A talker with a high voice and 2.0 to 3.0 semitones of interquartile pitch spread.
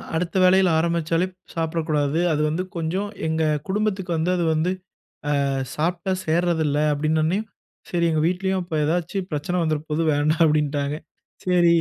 No: medium, 165 Hz; narrow, 2.5 semitones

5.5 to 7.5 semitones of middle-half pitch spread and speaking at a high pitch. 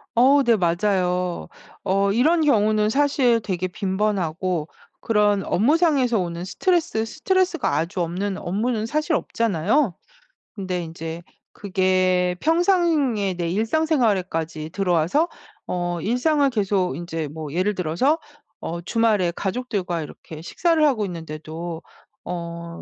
Yes: wide, 6.1 semitones; high, 195 Hz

